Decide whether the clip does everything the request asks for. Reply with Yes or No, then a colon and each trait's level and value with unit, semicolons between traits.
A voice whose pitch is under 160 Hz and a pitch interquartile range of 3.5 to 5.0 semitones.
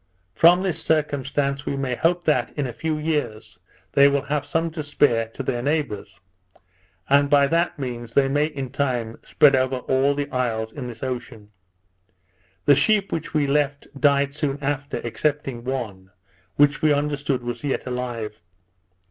No: medium, 140 Hz; average, 2.9 semitones